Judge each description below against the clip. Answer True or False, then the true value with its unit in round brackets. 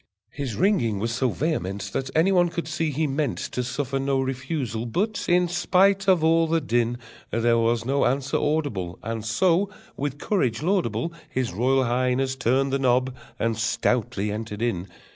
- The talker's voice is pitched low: True (130 Hz)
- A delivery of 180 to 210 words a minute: False (170 wpm)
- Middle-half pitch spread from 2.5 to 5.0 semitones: False (5.4 semitones)